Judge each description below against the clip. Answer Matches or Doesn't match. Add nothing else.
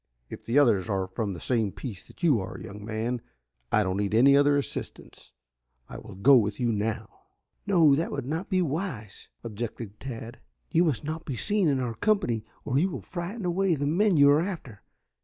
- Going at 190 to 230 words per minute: Matches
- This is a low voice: Matches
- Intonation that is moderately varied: Doesn't match